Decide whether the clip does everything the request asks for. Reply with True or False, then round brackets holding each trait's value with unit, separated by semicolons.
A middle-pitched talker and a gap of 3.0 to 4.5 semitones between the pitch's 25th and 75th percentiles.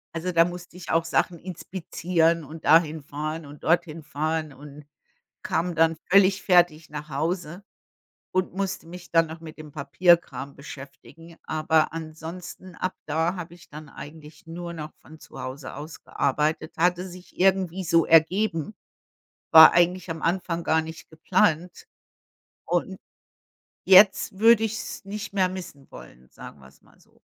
False (165 Hz; 2.6 semitones)